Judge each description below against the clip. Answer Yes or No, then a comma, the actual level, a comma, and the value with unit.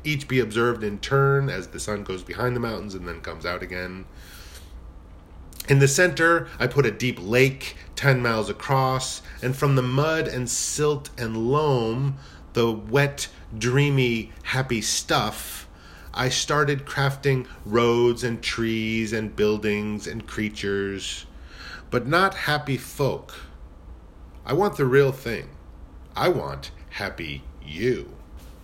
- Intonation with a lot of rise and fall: Yes, wide, 8.1 semitones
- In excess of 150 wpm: No, slow, 135 wpm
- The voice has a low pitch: Yes, low, 115 Hz